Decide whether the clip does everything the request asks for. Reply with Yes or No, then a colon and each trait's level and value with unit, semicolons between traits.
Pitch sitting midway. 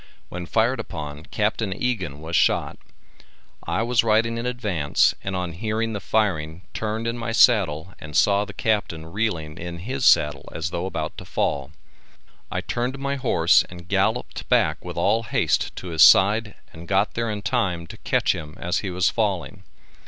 No: low, 100 Hz